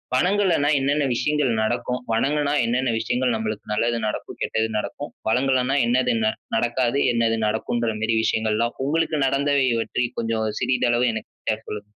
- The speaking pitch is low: Yes, low, 120 Hz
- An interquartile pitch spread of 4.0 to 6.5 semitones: No, average, 3.4 semitones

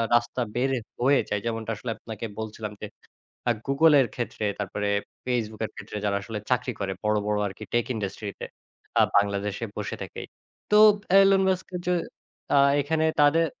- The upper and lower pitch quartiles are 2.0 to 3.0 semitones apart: No, average, 4.4 semitones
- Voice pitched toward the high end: No, low, 115 Hz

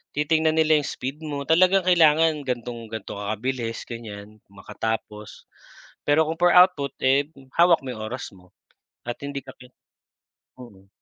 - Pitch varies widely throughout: Yes, wide, 5.8 semitones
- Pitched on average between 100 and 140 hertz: Yes, low, 135 Hz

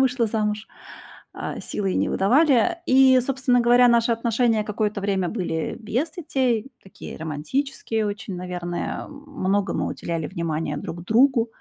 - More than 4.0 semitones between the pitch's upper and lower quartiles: Yes, average, 5.2 semitones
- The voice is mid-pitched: No, high, 225 Hz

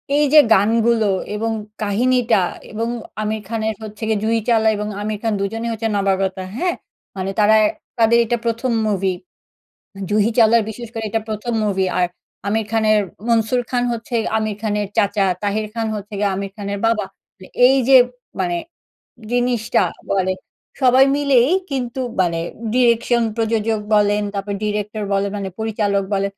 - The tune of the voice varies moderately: No, narrow, 2.3 semitones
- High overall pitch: Yes, high, 220 Hz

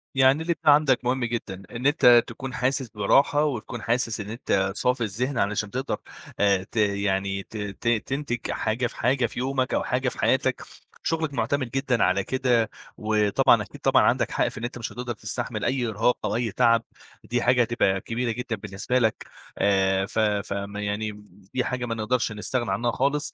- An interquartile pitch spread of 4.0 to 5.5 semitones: No, average, 3.3 semitones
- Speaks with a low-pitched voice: Yes, low, 120 Hz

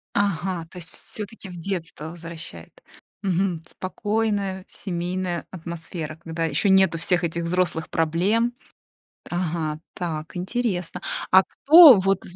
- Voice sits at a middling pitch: Yes, medium, 180 Hz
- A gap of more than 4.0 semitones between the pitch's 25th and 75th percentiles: No, average, 2.7 semitones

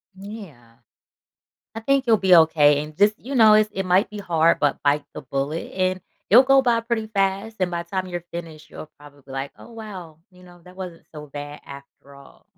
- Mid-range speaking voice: Yes, medium, 180 Hz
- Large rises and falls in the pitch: Yes, wide, 6.0 semitones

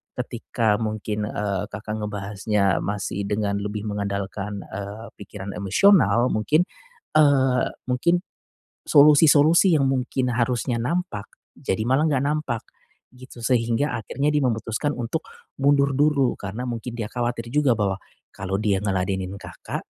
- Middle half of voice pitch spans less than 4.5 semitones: No, average, 4.9 semitones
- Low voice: Yes, low, 115 Hz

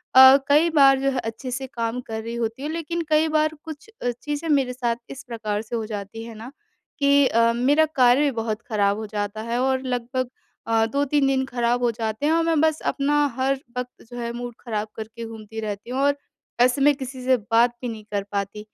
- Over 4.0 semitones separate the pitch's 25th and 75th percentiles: No, average, 3.6 semitones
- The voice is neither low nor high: No, high, 245 Hz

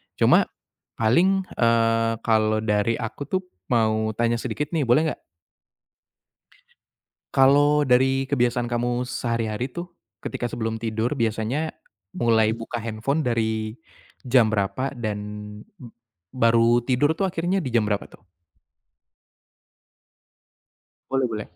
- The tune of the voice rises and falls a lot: No, average, 3.2 semitones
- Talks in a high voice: No, low, 120 Hz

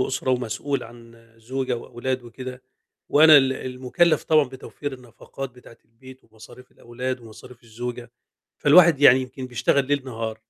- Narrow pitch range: Yes, narrow, 2.1 semitones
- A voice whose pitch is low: Yes, low, 125 Hz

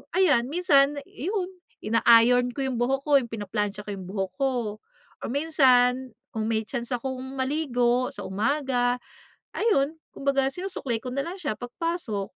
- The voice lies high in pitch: Yes, very high, 255 Hz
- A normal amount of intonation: Yes, average, 3.5 semitones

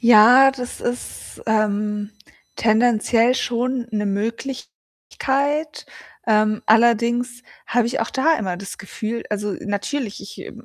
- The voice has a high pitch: Yes, high, 230 Hz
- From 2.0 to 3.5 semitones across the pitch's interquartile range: Yes, average, 2.9 semitones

